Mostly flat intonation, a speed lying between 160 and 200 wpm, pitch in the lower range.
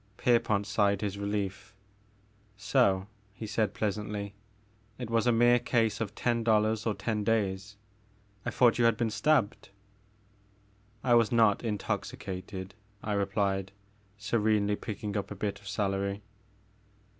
No: narrow, 2.1 semitones; slow, 135 wpm; low, 105 Hz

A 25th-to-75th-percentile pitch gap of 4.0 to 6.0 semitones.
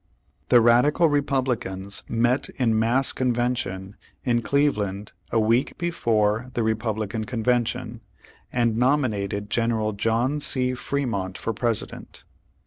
No: average, 2.8 semitones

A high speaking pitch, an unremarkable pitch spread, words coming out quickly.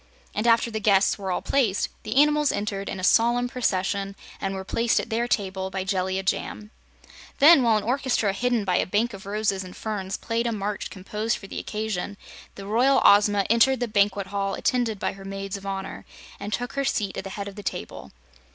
Yes: high, 205 Hz; average, 3.0 semitones; fast, 210 wpm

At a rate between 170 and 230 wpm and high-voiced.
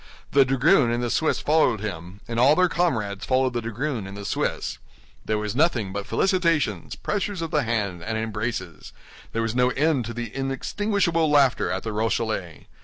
No: average, 180 wpm; low, 120 Hz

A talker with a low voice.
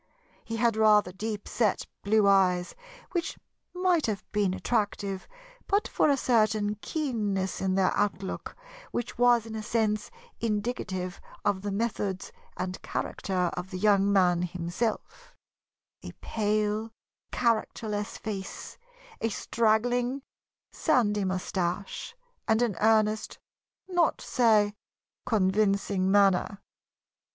No: high, 210 Hz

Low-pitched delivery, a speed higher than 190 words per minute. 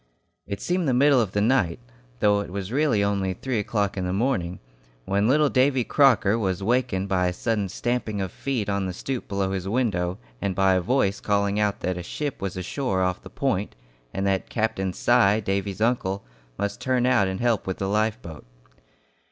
Yes: low, 100 Hz; average, 200 wpm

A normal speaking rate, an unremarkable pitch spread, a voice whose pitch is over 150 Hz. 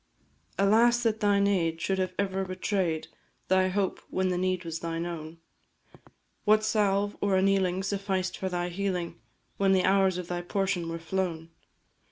No: average, 160 wpm; narrow, 2.1 semitones; high, 190 Hz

